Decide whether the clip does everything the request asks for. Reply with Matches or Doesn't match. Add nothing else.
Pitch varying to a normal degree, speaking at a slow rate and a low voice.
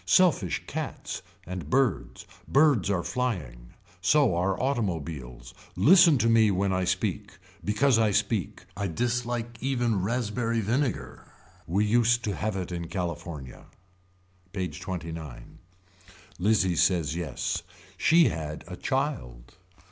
Doesn't match